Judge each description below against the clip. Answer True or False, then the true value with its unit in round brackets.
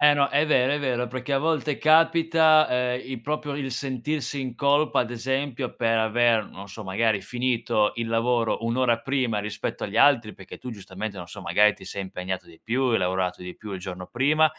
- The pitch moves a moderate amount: True (4.9 semitones)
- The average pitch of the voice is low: True (120 Hz)